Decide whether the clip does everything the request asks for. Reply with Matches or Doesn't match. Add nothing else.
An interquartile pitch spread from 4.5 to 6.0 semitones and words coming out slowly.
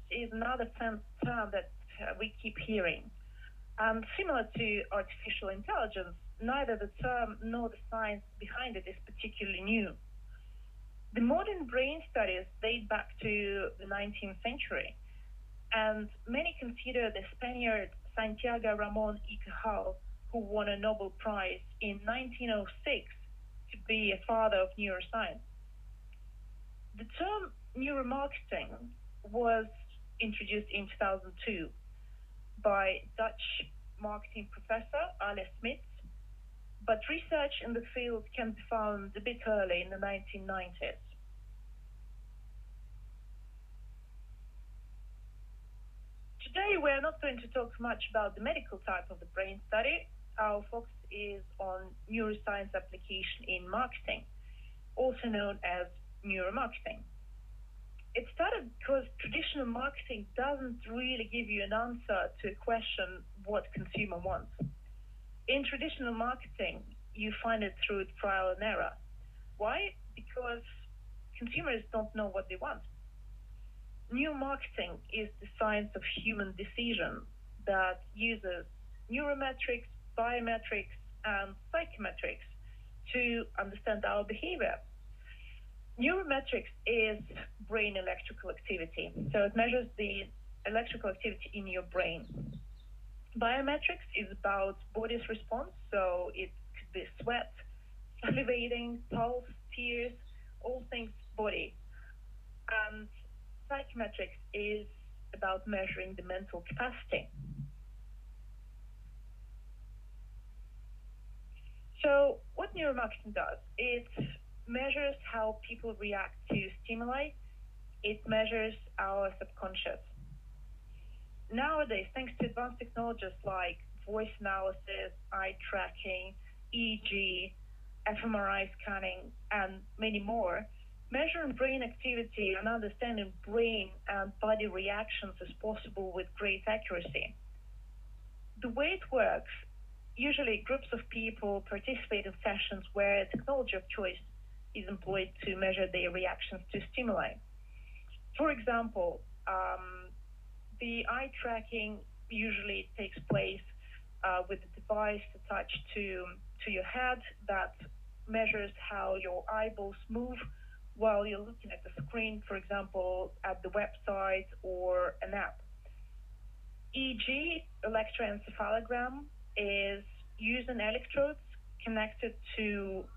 Doesn't match